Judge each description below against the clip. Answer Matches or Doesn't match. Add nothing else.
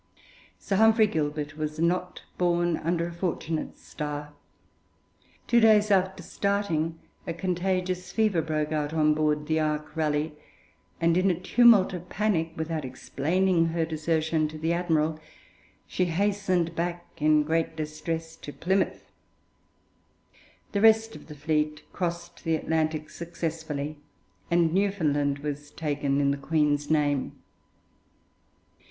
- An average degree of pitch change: Matches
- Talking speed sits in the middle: Doesn't match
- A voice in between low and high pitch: Matches